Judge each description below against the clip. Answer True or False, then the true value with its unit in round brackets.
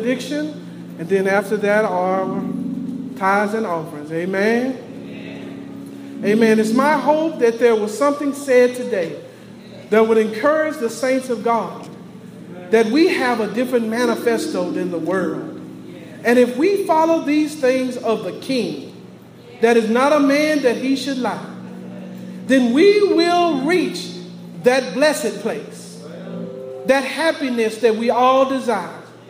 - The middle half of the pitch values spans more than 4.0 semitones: True (5.0 semitones)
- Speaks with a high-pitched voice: True (235 Hz)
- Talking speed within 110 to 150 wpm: True (135 wpm)